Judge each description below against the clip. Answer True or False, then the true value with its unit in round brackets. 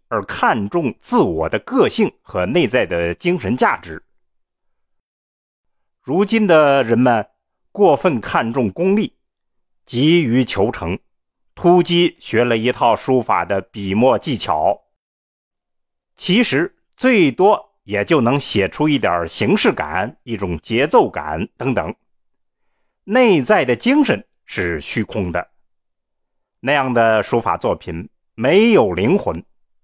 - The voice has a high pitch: False (120 Hz)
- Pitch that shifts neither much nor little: False (8.3 semitones)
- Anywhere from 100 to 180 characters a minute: True (170 characters per minute)